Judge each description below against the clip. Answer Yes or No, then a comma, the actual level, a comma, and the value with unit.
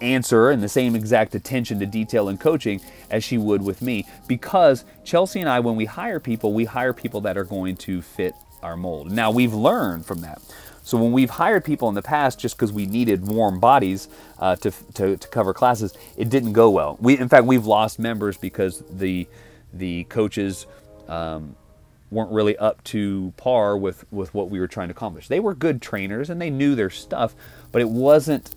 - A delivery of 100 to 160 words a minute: No, fast, 205 wpm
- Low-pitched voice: Yes, low, 110 Hz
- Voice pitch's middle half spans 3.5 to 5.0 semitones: Yes, average, 4.1 semitones